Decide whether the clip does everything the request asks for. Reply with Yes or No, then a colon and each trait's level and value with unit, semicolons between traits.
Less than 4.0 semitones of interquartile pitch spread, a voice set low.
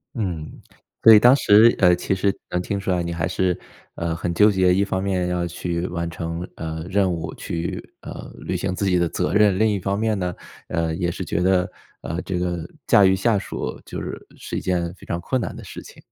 Yes: narrow, 2.5 semitones; very low, 90 Hz